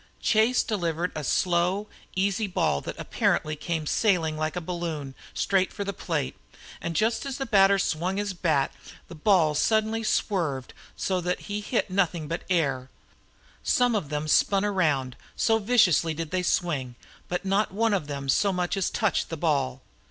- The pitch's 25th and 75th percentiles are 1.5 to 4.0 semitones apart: No, average, 4.6 semitones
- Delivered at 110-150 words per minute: No, average, 175 wpm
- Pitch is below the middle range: No, medium, 180 Hz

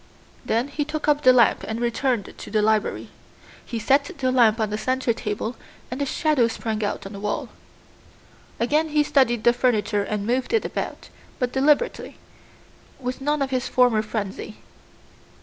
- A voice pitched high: Yes, high, 245 Hz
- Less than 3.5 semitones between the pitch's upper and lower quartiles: No, average, 4.1 semitones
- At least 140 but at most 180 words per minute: Yes, average, 170 wpm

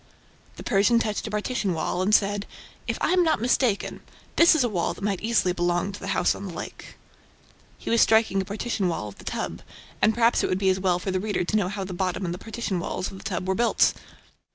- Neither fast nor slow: No, fast, 245 wpm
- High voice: Yes, high, 200 Hz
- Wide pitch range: No, average, 3.2 semitones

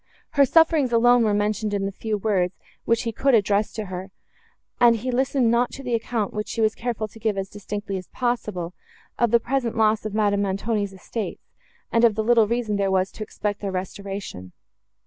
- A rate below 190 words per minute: No, fast, 205 wpm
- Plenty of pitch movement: No, average, 2.8 semitones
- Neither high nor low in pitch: No, high, 215 Hz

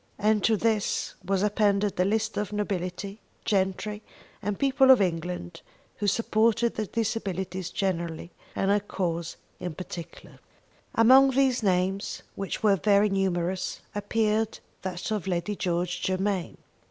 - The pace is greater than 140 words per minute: No, slow, 135 wpm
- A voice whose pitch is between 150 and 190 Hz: No, high, 200 Hz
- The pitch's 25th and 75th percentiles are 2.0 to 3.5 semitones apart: Yes, average, 2.9 semitones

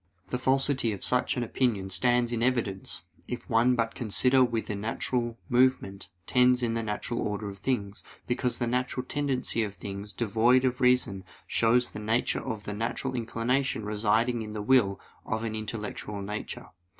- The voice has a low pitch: Yes, low, 115 Hz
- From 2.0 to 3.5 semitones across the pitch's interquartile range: Yes, average, 3.1 semitones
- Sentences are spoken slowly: No, average, 165 wpm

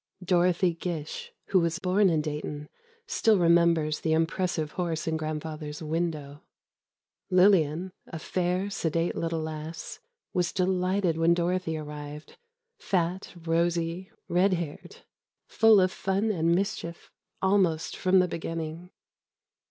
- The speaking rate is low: Yes, slow, 115 wpm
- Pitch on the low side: No, medium, 170 Hz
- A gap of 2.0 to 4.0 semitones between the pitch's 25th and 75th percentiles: Yes, narrow, 2.6 semitones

